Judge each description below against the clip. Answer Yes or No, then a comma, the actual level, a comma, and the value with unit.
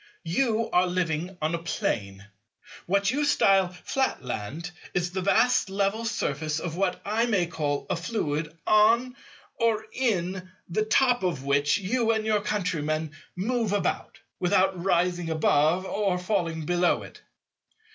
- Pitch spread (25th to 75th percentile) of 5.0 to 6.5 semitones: No, average, 4.6 semitones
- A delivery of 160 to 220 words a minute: No, slow, 135 wpm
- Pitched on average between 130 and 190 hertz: Yes, medium, 185 Hz